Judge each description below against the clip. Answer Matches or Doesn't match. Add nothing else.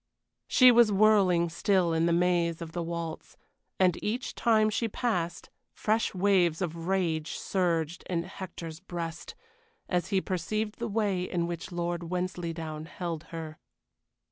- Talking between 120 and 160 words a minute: Matches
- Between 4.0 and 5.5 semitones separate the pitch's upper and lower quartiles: Doesn't match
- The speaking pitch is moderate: Matches